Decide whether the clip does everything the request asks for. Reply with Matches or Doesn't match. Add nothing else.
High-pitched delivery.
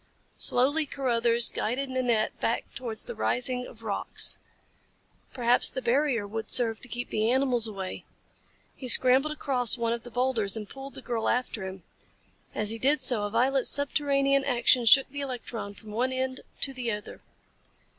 Matches